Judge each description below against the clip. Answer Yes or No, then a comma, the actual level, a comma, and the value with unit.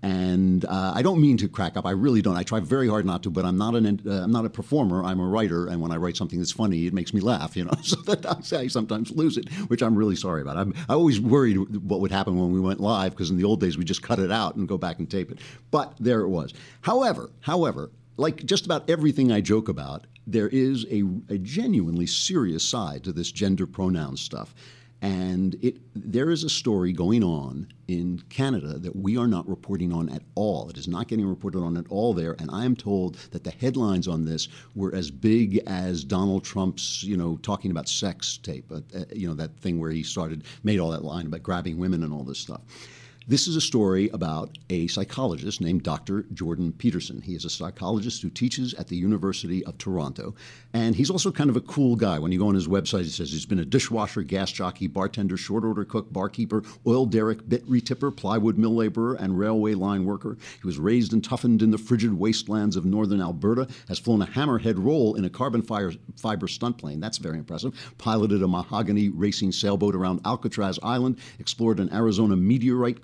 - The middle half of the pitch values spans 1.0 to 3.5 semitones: No, average, 4.6 semitones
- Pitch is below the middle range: Yes, low, 105 Hz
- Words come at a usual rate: No, fast, 220 wpm